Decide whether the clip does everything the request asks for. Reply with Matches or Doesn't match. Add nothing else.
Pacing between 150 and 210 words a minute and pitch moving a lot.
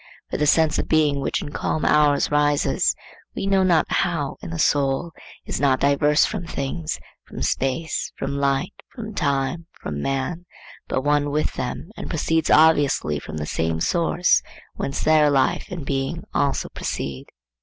Doesn't match